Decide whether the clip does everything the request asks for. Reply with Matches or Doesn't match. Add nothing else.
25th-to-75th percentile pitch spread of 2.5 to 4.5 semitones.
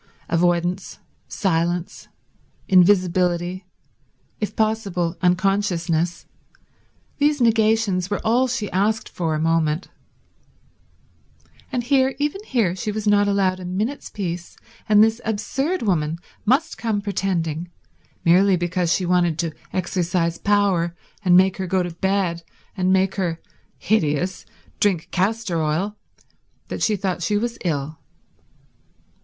Matches